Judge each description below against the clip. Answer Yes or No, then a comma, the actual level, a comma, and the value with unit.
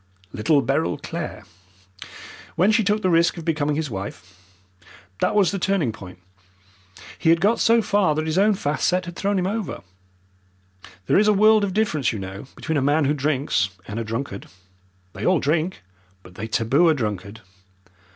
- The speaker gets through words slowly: No, average, 180 wpm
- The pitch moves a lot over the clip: Yes, wide, 7.8 semitones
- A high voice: No, medium, 155 Hz